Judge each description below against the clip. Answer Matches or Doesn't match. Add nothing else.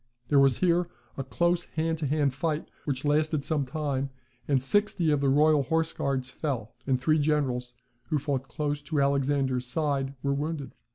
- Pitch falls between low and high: Matches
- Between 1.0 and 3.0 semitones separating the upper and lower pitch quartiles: Matches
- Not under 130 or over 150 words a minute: Doesn't match